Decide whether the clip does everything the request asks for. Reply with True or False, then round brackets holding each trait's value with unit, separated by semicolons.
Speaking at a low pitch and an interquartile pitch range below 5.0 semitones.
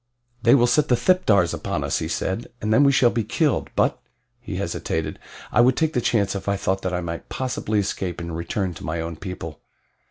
False (100 Hz; 5.6 semitones)